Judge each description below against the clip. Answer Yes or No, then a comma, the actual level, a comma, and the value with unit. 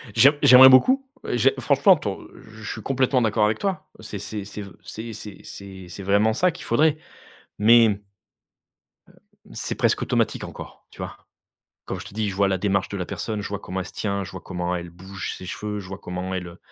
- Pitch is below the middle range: Yes, low, 105 Hz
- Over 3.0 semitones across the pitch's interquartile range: Yes, average, 3.7 semitones